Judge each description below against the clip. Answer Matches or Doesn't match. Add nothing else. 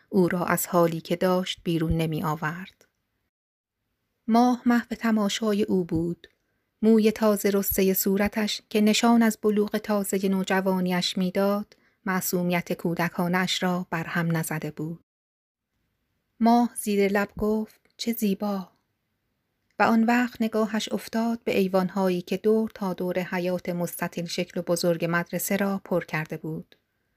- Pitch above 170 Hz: Matches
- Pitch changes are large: Doesn't match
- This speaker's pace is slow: Doesn't match